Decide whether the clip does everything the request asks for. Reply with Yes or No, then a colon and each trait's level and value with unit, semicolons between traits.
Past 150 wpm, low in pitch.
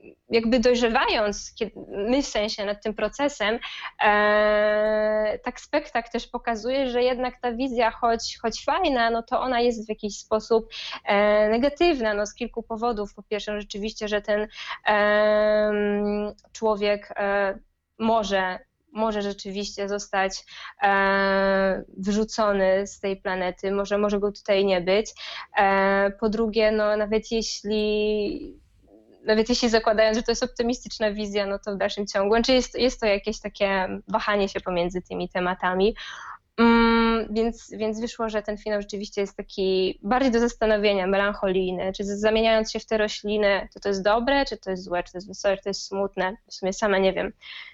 No: fast, 160 wpm; high, 210 Hz